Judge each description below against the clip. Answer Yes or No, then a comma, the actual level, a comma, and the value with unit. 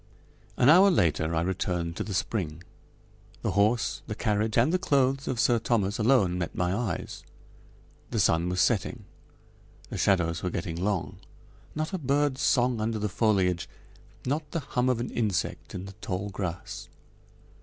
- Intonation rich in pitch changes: Yes, wide, 5.7 semitones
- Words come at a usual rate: Yes, average, 165 wpm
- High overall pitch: No, low, 105 Hz